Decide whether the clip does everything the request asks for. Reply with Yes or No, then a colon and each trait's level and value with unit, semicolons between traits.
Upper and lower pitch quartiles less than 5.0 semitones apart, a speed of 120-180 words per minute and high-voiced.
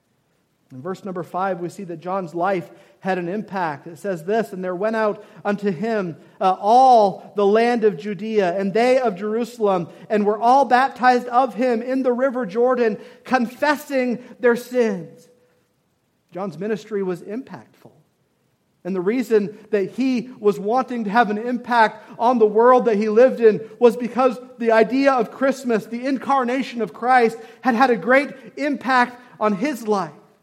Yes: average, 3.6 semitones; average, 165 wpm; high, 225 Hz